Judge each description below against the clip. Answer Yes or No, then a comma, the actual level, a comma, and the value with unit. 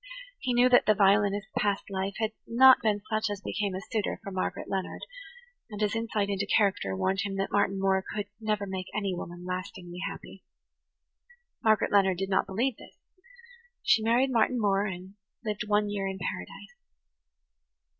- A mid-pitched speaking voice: No, high, 200 Hz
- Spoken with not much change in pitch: Yes, narrow, 2.1 semitones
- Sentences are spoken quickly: No, average, 170 wpm